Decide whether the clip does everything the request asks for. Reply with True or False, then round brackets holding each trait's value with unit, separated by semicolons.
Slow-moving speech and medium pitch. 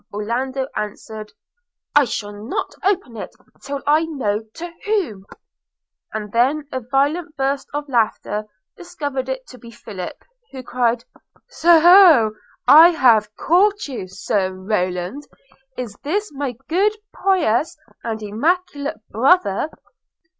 False (125 wpm; 260 Hz)